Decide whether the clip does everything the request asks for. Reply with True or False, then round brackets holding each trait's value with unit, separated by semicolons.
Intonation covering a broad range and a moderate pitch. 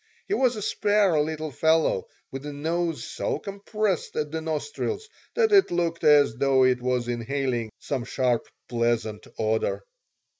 True (5.9 semitones; 150 Hz)